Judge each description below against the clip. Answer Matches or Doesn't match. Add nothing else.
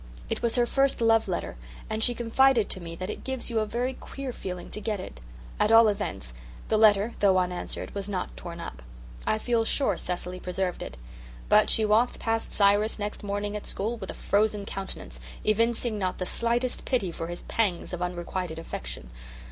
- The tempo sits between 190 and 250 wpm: Matches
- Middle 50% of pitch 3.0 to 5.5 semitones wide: Matches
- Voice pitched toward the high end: Matches